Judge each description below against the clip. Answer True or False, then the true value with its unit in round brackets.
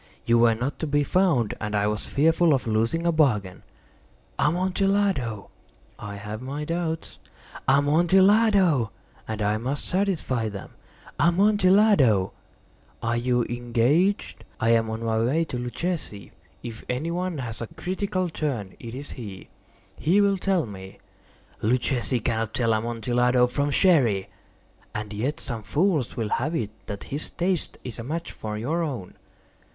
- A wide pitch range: True (7.0 semitones)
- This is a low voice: True (130 Hz)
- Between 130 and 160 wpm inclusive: True (145 wpm)